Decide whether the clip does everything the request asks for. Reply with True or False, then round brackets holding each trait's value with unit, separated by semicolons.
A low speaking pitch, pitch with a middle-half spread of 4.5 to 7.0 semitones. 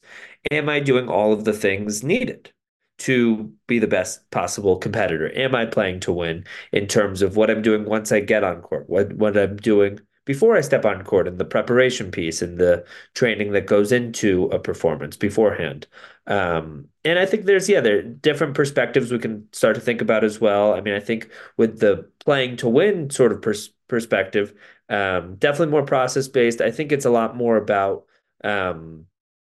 True (110 Hz; 4.9 semitones)